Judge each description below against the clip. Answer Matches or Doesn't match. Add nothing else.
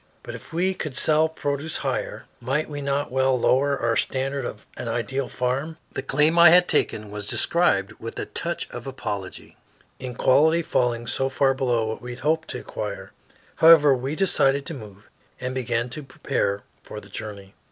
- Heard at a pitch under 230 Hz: Matches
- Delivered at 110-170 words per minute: Doesn't match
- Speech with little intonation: Doesn't match